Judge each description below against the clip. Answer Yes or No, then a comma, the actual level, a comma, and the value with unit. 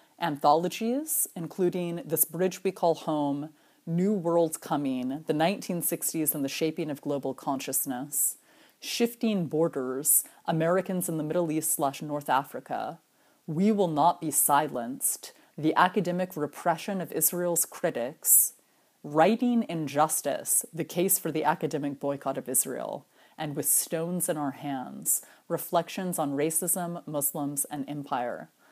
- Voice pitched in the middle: Yes, medium, 160 Hz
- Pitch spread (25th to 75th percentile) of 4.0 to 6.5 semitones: No, average, 3.2 semitones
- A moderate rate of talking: No, slow, 125 wpm